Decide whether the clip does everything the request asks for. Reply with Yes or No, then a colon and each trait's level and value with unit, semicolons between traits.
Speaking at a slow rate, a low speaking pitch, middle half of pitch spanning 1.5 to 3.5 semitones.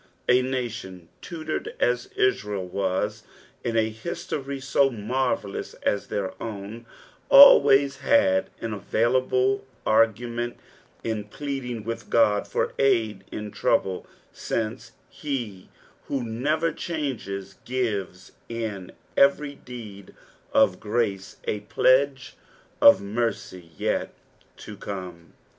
No: slow, 110 wpm; low, 115 Hz; average, 4.4 semitones